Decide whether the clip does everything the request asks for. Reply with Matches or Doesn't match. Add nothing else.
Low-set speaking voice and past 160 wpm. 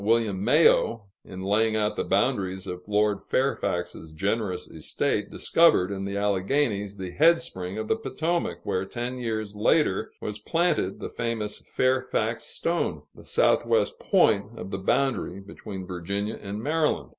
Doesn't match